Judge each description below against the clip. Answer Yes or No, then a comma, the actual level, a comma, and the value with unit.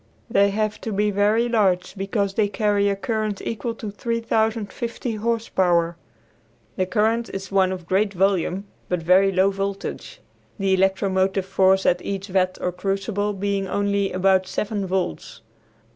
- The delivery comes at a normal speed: Yes, average, 150 wpm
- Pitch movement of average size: No, narrow, 1.9 semitones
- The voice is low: No, high, 195 Hz